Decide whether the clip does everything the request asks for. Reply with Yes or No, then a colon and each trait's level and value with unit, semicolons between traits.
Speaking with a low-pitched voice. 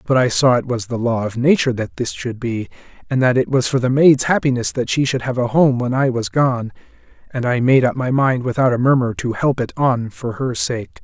Yes: low, 125 Hz